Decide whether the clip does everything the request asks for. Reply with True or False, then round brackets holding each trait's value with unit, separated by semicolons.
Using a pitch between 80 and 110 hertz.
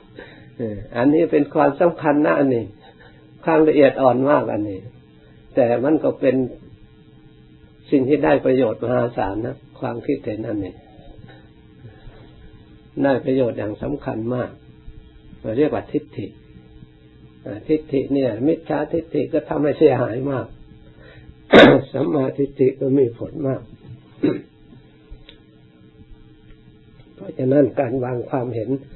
False (125 Hz)